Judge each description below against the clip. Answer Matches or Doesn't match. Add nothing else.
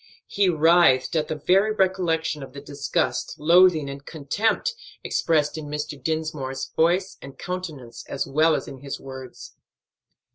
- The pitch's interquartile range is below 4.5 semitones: Matches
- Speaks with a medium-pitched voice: Matches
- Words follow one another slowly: Doesn't match